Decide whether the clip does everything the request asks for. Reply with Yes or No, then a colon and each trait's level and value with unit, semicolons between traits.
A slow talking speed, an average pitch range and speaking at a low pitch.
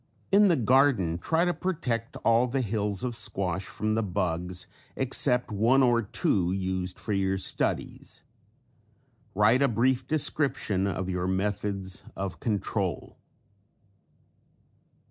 Yes: slow, 125 wpm; average, 5.0 semitones; low, 105 Hz